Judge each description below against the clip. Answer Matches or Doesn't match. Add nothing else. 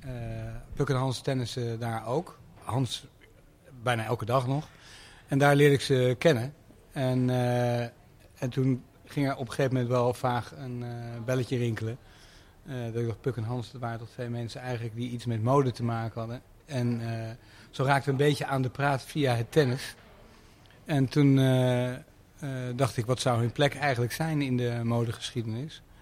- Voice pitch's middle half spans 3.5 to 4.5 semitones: Doesn't match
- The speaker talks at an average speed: Matches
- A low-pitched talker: Matches